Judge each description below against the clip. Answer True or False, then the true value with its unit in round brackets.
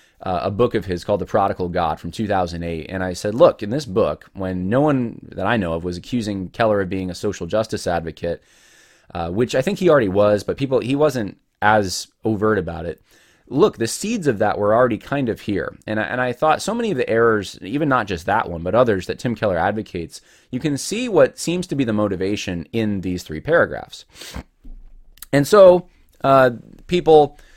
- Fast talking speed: True (210 wpm)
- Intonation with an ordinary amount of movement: False (6.2 semitones)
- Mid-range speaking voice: False (110 Hz)